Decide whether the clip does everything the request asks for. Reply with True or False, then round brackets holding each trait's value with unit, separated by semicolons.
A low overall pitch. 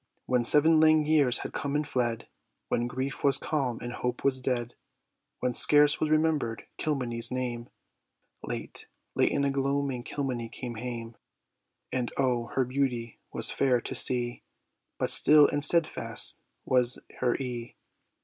True (130 Hz)